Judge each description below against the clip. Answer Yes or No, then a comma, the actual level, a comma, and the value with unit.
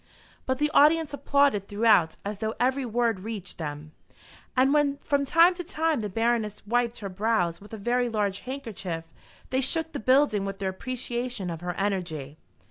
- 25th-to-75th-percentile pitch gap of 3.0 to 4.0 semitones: No, average, 5.3 semitones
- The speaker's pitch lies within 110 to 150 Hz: No, high, 225 Hz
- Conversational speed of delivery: Yes, average, 175 wpm